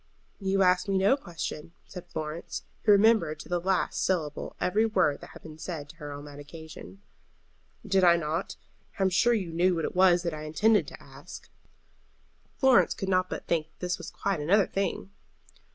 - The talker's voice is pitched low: No, medium, 180 Hz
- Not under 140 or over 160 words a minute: No, average, 195 wpm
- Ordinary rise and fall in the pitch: Yes, average, 3.6 semitones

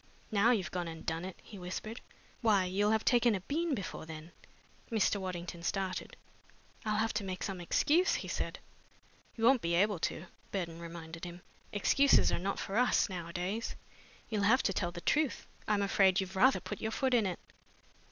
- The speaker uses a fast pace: No, average, 185 wpm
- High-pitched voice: Yes, high, 195 Hz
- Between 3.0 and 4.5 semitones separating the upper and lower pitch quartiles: Yes, average, 4.1 semitones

